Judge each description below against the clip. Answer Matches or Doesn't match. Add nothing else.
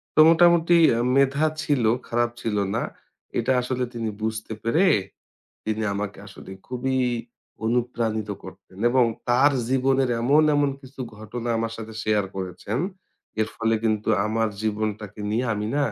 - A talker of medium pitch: Doesn't match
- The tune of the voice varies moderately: Matches